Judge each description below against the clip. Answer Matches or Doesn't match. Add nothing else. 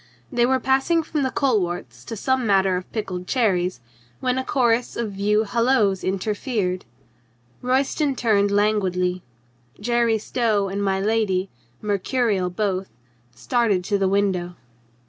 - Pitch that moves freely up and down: Doesn't match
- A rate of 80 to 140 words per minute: Matches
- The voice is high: Matches